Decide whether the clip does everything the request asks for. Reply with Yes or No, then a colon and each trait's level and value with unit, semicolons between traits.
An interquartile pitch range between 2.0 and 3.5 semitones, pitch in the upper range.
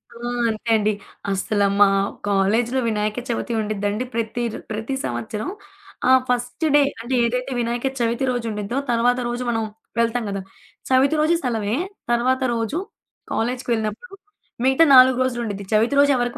Yes: average, 2.8 semitones; high, 235 Hz